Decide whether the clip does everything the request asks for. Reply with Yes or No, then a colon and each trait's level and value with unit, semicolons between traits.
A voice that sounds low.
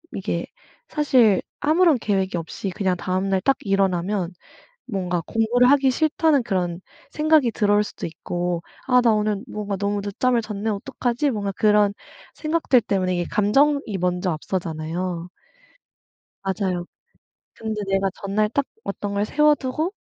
No: high, 205 Hz